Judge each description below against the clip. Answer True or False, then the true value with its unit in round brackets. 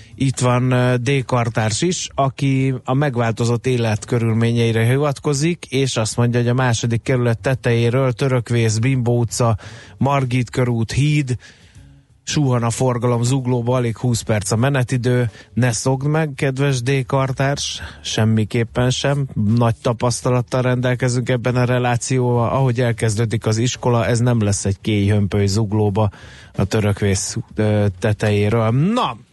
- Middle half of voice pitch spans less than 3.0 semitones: True (2.6 semitones)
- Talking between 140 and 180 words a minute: False (125 wpm)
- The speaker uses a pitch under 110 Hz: False (120 Hz)